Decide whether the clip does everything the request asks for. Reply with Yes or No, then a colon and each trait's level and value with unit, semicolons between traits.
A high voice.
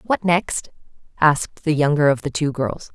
No: medium, 150 Hz